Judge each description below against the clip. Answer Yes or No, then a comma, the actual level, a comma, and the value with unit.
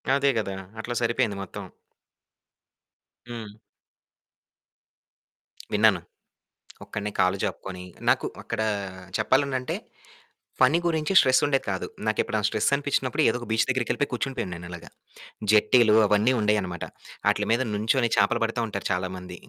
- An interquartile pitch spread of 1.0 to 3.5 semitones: No, average, 4.1 semitones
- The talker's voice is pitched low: Yes, low, 110 Hz